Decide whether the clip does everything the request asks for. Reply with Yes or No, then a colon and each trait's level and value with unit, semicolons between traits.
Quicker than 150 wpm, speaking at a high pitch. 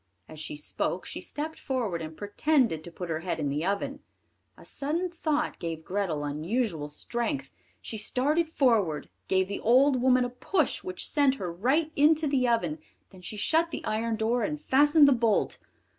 Yes: average, 180 wpm; high, 235 Hz